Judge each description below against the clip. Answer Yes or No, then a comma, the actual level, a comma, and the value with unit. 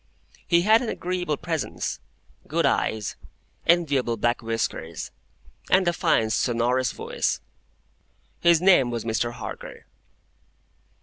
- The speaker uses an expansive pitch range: Yes, wide, 6.9 semitones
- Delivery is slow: Yes, slow, 110 wpm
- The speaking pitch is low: Yes, low, 130 Hz